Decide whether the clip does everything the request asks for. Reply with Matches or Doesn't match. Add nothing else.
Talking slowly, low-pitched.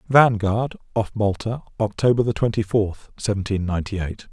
Matches